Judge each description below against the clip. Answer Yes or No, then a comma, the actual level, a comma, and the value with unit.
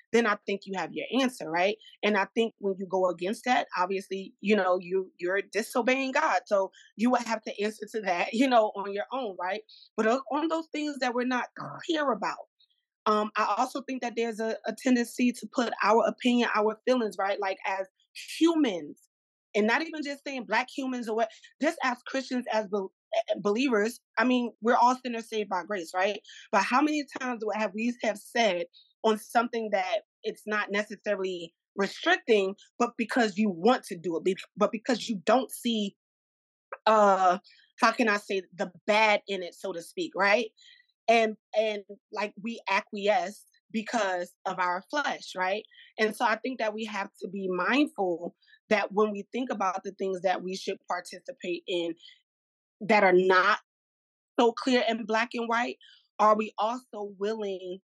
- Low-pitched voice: No, high, 215 Hz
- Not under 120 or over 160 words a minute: No, average, 180 wpm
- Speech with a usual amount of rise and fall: Yes, average, 4.0 semitones